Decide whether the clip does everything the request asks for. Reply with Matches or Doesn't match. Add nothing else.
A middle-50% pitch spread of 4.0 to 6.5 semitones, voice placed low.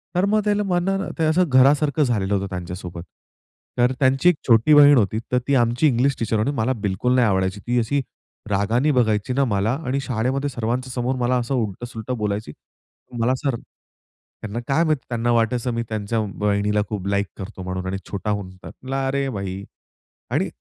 Matches